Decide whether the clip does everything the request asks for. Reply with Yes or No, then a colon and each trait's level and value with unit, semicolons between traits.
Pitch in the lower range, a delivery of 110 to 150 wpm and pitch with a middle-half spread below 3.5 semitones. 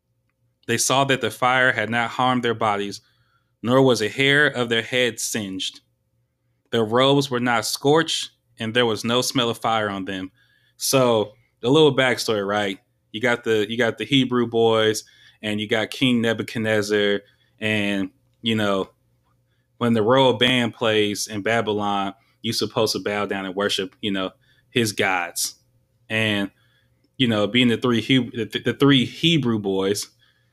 No: low, 115 Hz; average, 165 wpm; average, 3.0 semitones